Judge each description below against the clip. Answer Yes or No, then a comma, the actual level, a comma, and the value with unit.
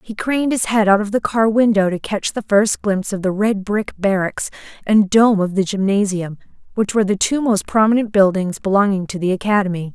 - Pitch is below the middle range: No, high, 205 Hz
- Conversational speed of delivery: No, fast, 210 wpm